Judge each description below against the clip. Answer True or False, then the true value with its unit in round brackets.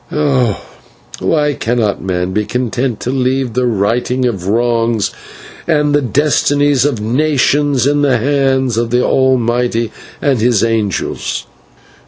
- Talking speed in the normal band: False (130 wpm)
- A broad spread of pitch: False (3.4 semitones)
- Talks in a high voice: False (125 Hz)